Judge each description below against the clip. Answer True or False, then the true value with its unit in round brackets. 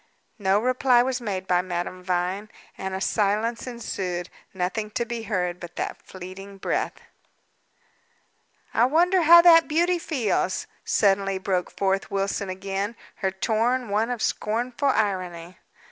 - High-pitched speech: True (200 Hz)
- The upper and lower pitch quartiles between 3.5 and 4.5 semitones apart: True (4.2 semitones)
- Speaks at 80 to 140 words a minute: True (135 wpm)